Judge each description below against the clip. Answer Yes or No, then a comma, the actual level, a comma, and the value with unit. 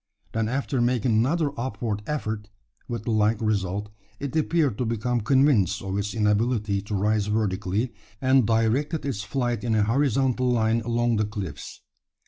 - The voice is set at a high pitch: No, low, 115 Hz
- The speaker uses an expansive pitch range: No, average, 3.4 semitones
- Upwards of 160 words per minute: No, average, 155 wpm